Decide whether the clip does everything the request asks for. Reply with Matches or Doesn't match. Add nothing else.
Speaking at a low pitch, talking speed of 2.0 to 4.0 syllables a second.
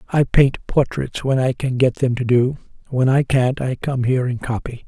Doesn't match